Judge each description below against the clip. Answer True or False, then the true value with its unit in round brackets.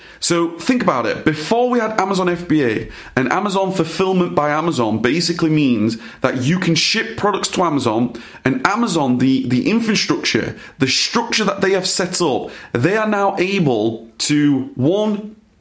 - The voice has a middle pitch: True (170 Hz)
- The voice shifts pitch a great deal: True (6.7 semitones)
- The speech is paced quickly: False (160 wpm)